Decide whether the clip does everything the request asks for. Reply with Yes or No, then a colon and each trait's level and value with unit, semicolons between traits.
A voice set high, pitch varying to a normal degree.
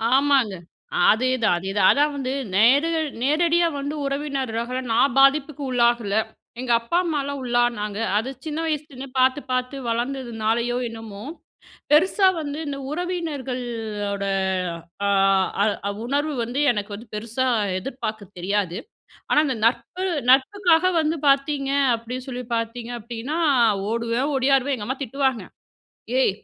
Yes: very high, 255 Hz; average, 3.8 semitones